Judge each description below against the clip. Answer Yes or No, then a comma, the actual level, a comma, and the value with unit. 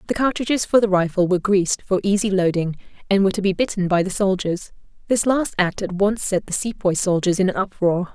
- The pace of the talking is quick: Yes, fast, 220 wpm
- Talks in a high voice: Yes, high, 195 Hz